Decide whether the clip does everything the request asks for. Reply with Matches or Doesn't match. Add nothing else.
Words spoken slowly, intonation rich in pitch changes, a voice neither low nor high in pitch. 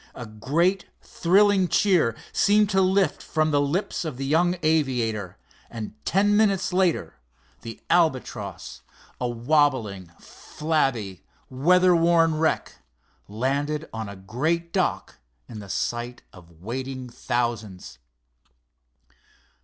Matches